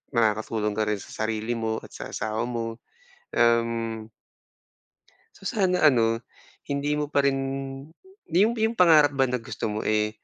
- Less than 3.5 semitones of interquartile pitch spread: No, average, 4.8 semitones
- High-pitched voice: No, low, 115 Hz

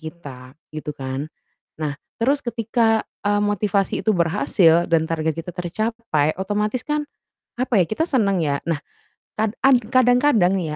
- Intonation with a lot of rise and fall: Yes, wide, 6.0 semitones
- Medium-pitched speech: No, high, 200 Hz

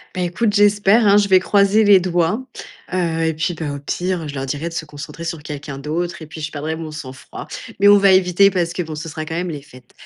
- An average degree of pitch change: Yes, average, 3.7 semitones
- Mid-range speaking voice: Yes, medium, 170 Hz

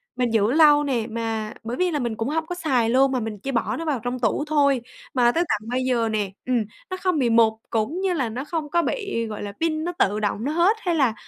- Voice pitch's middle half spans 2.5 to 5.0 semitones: No, wide, 5.6 semitones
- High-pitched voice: Yes, very high, 255 Hz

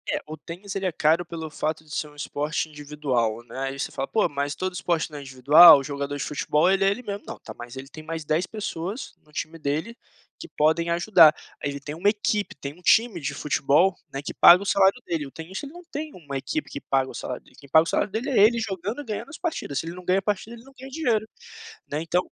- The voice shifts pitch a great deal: Yes, wide, 5.7 semitones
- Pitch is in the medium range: Yes, medium, 165 Hz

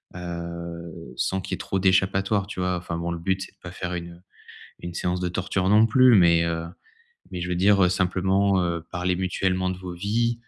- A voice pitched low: Yes, very low, 90 Hz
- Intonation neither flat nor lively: No, narrow, 1.9 semitones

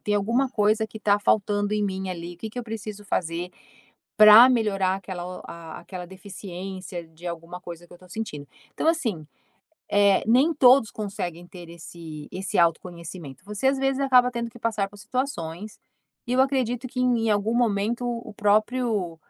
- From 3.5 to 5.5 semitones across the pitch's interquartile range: Yes, average, 4.8 semitones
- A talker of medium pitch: No, high, 205 Hz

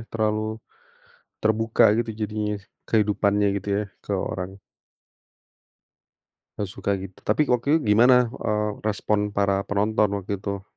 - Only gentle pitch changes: Yes, narrow, 1.4 semitones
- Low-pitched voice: Yes, low, 105 Hz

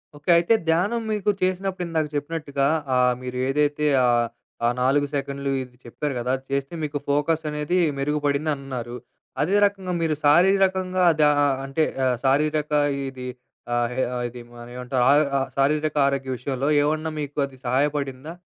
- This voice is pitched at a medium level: Yes, medium, 145 Hz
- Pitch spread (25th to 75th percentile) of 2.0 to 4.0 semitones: Yes, average, 3.2 semitones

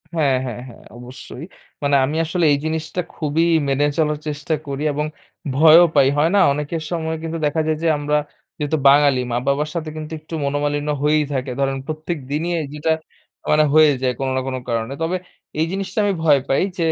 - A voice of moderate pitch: Yes, medium, 150 Hz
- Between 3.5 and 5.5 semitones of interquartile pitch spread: No, narrow, 2.4 semitones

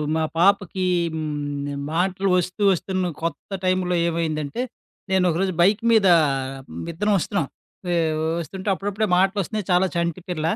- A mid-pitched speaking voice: Yes, medium, 180 Hz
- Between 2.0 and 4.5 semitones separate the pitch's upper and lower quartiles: Yes, average, 2.9 semitones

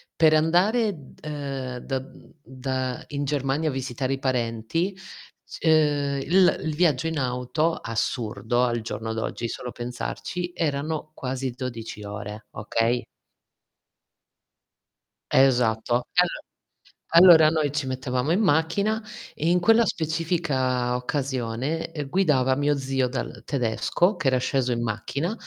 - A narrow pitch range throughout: No, average, 4.3 semitones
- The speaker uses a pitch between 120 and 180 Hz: Yes, low, 135 Hz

